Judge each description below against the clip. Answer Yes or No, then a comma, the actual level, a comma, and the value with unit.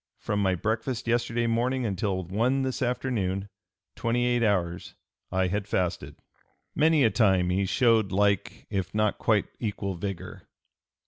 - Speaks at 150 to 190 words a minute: No, average, 140 wpm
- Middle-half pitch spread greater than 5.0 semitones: No, average, 3.8 semitones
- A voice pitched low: Yes, low, 105 Hz